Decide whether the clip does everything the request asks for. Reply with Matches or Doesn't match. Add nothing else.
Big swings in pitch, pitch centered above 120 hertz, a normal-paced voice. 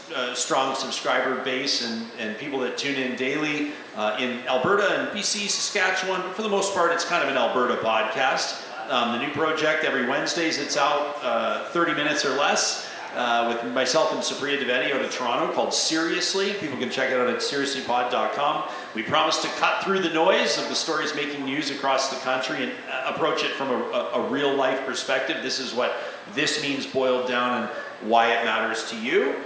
Doesn't match